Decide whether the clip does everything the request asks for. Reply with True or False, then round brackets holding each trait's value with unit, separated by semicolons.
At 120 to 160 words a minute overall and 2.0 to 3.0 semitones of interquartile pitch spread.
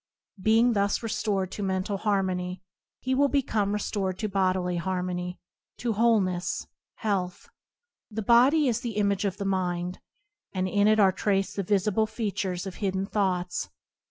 True (150 wpm; 2.7 semitones)